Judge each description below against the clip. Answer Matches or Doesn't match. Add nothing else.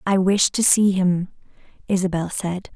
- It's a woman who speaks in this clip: Matches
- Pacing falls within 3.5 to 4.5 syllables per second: Matches